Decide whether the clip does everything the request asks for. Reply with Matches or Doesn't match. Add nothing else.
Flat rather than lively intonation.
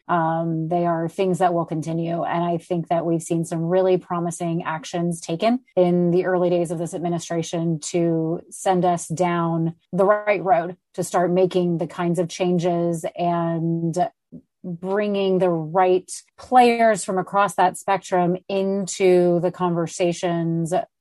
Matches